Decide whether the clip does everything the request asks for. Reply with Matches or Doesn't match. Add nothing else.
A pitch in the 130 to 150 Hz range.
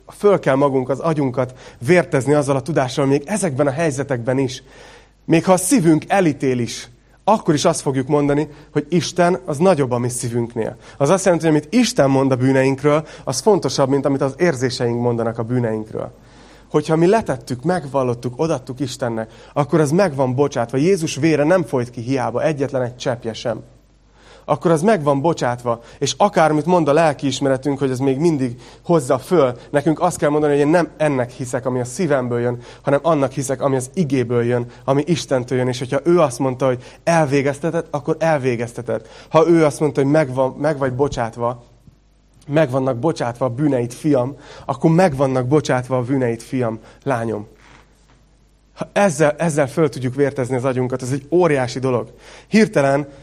Matches